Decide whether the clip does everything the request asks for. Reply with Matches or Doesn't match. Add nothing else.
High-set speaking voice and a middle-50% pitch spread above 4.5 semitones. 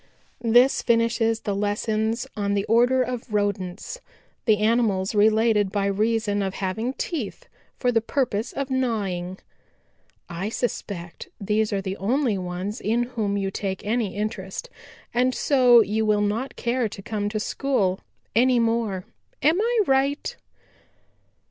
Doesn't match